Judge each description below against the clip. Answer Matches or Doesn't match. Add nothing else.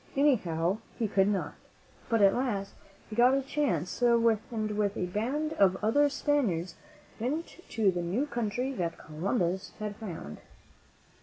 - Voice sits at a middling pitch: Doesn't match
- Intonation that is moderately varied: Matches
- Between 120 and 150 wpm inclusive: Matches